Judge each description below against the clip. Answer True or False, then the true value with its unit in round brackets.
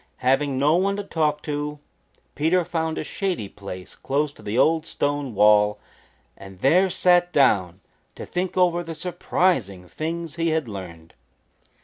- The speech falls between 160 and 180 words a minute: False (150 wpm)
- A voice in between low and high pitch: True (150 Hz)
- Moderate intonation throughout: False (8.3 semitones)